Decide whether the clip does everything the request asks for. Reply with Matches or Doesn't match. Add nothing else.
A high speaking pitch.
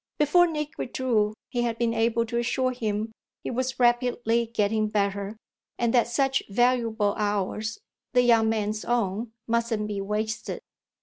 Matches